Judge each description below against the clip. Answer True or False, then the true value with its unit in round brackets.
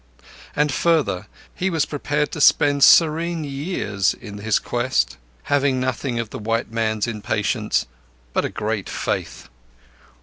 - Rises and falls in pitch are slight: False (5.6 semitones)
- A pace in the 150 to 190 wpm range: False (135 wpm)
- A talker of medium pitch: False (125 Hz)